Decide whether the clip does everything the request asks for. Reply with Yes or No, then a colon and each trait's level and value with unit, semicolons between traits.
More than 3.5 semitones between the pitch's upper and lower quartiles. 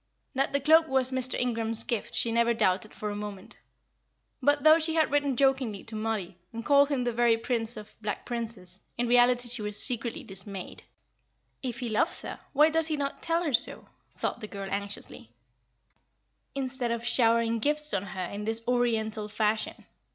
Yes: average, 3.9 semitones